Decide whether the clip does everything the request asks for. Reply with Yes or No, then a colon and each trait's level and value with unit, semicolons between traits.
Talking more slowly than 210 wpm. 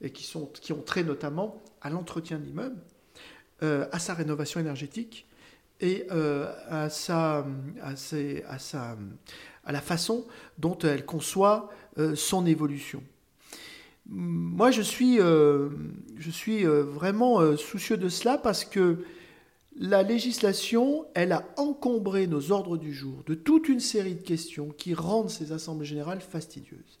Yes: average, 150 wpm